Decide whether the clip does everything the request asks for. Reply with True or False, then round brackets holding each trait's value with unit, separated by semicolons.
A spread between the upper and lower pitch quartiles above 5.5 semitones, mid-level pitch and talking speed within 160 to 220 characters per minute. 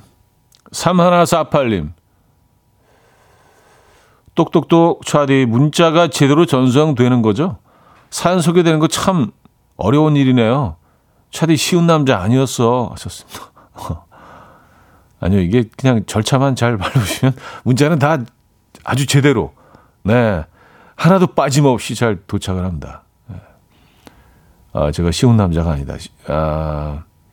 False (6.9 semitones; 125 Hz; 215 characters per minute)